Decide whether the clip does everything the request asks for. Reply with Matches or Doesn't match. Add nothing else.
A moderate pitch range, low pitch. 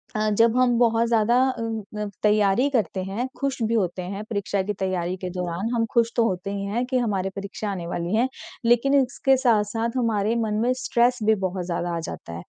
Doesn't match